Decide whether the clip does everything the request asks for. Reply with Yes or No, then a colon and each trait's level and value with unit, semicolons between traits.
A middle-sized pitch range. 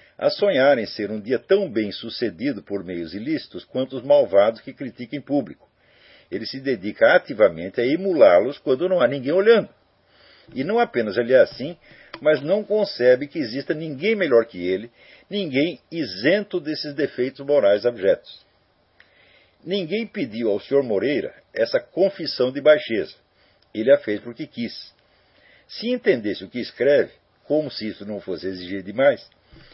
No: wide, 6.9 semitones